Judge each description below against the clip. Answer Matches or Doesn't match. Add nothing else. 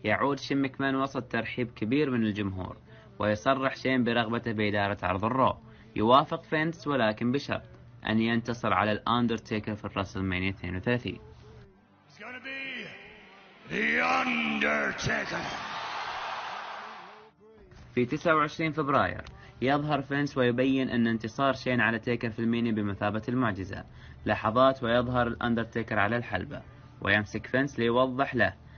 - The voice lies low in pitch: Matches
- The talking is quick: Doesn't match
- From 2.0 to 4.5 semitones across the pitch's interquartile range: Matches